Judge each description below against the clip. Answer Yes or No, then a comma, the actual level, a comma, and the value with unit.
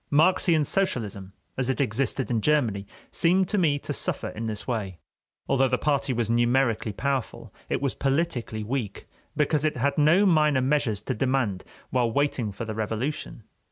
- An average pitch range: Yes, average, 4.8 semitones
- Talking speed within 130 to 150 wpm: No, average, 165 wpm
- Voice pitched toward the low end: Yes, low, 130 Hz